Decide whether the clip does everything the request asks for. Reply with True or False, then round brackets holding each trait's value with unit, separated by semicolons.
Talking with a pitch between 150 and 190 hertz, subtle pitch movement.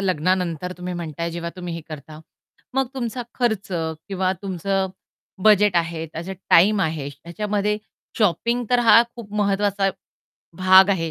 False (185 Hz; 3.7 semitones)